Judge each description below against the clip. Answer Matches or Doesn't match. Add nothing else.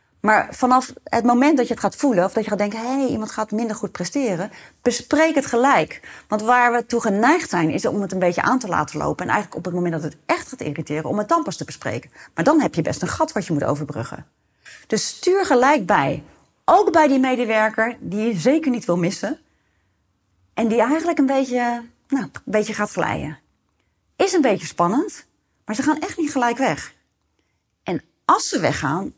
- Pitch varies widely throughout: Matches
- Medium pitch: Doesn't match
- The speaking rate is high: Matches